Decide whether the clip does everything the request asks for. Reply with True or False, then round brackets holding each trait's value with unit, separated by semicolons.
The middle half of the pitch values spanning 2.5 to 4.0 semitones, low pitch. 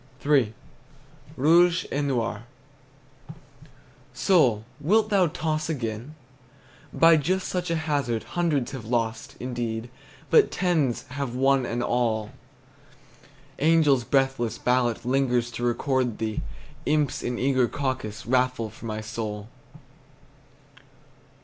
False (4.5 semitones; 130 Hz)